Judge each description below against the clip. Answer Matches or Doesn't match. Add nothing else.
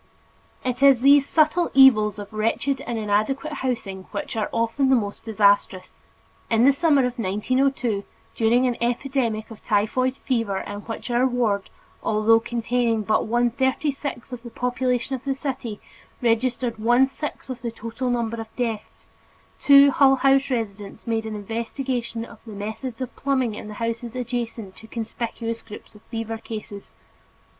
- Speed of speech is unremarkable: Matches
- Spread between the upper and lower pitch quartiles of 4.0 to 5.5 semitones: Doesn't match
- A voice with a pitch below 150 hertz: Doesn't match